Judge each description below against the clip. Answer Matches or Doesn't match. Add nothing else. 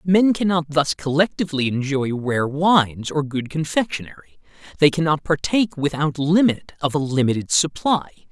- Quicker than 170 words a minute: Doesn't match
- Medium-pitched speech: Matches